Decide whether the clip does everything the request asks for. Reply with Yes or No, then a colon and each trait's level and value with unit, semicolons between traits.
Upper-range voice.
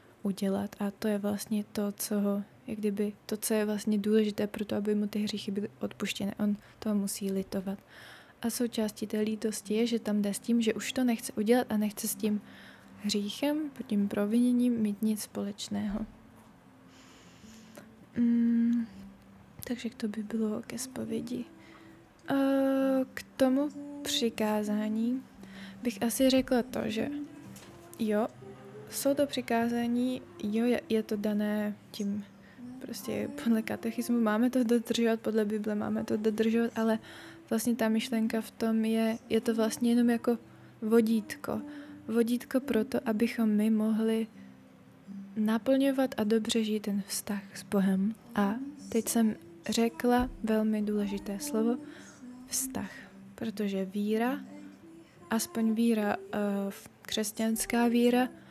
Yes: high, 220 Hz